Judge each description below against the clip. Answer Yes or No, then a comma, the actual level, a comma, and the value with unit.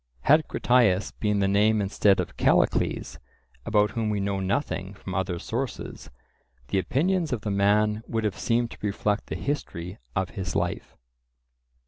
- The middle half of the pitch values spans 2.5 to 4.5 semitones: Yes, average, 2.9 semitones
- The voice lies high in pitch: No, low, 105 Hz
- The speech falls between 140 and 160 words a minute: Yes, average, 155 wpm